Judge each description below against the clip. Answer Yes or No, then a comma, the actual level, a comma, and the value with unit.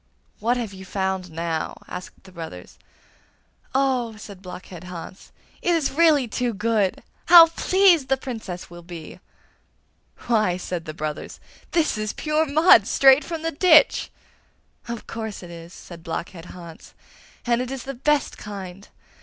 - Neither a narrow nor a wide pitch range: No, wide, 7.2 semitones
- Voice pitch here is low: No, high, 215 Hz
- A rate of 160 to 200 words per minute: No, average, 150 wpm